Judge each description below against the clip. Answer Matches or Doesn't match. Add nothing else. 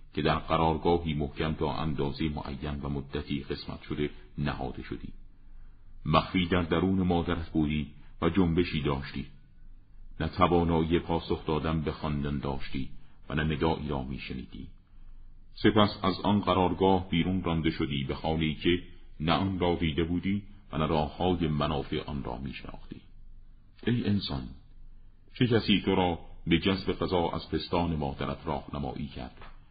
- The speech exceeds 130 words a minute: Matches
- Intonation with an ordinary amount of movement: Matches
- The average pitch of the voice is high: Doesn't match